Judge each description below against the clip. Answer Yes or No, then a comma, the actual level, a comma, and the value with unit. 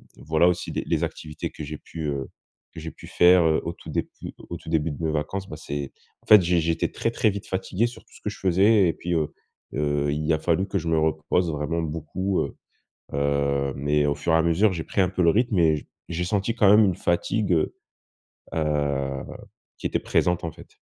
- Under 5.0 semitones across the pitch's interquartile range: Yes, average, 3.7 semitones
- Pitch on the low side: Yes, very low, 80 Hz